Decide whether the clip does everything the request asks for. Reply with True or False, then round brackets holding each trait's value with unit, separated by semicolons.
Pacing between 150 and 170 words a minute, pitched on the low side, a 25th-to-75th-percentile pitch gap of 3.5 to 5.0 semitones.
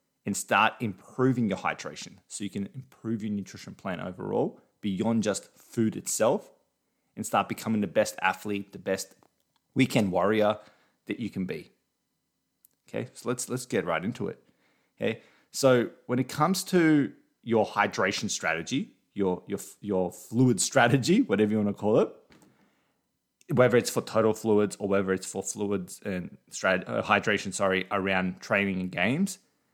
True (155 wpm; 105 Hz; 4.0 semitones)